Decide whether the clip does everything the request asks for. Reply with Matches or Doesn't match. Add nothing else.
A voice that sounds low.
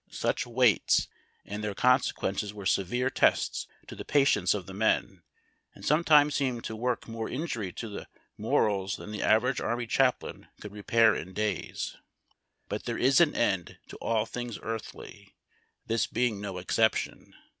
Matches